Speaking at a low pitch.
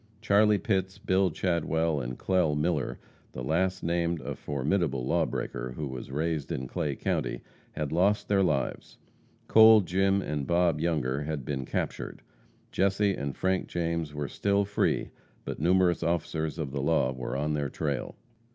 Yes: very low, 80 Hz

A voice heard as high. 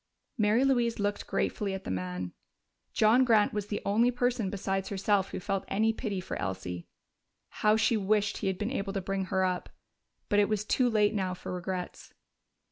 Yes: high, 205 Hz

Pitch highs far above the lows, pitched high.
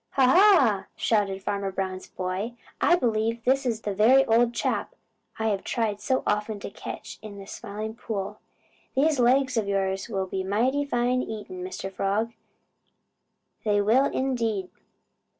No: average, 3.9 semitones; high, 220 Hz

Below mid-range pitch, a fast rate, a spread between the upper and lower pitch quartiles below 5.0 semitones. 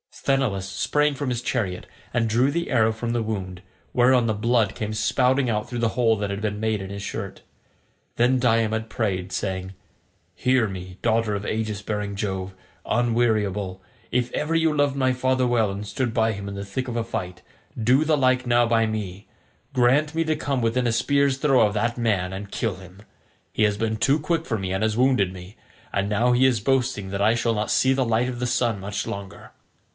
Yes: low, 115 Hz; fast, 210 wpm; average, 3.8 semitones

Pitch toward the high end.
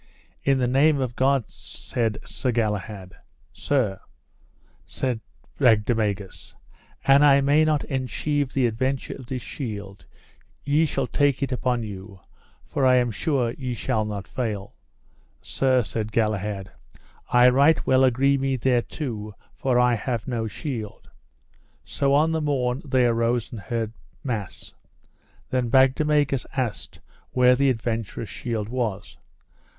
No: low, 125 Hz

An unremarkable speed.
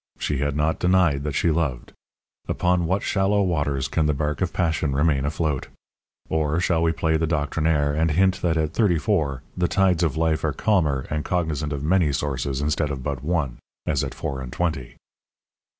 Yes: average, 190 wpm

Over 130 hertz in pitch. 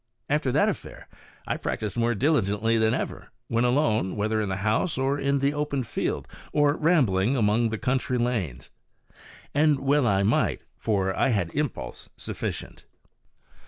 No: low, 120 Hz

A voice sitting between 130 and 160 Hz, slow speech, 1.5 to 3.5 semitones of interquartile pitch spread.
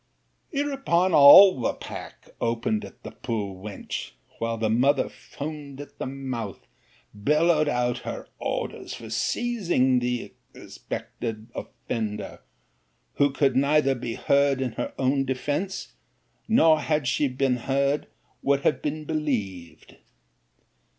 No: low, 135 Hz; slow, 125 wpm; average, 4.1 semitones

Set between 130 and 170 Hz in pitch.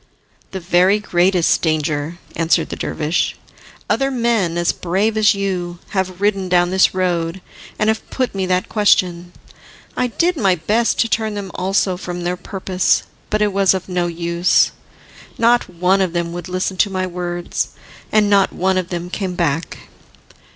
No: medium, 185 Hz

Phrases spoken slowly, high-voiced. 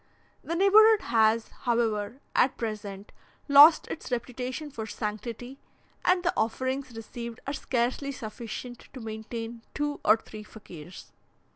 Yes: slow, 125 wpm; high, 235 Hz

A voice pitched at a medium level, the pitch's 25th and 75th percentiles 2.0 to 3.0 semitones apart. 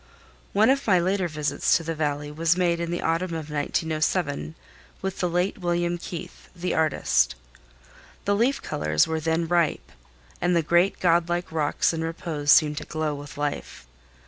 Yes: medium, 165 Hz; narrow, 2.5 semitones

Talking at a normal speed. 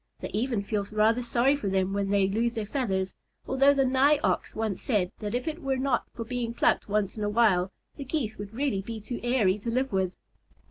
No: fast, 225 wpm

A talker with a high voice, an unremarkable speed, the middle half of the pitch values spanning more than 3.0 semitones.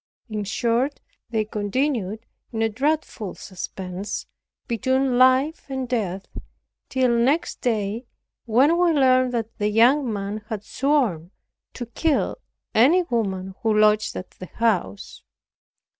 No: high, 230 Hz; slow, 125 wpm; average, 4.0 semitones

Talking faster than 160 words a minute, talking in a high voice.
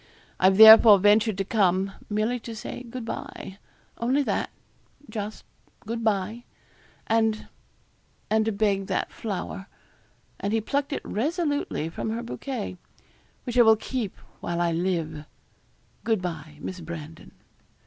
No: slow, 135 wpm; high, 215 Hz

